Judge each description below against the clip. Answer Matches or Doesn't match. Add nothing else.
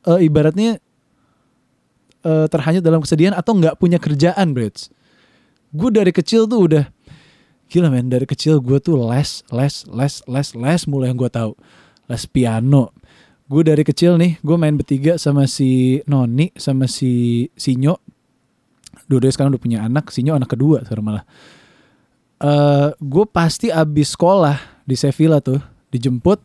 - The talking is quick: Doesn't match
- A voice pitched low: Doesn't match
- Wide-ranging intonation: Doesn't match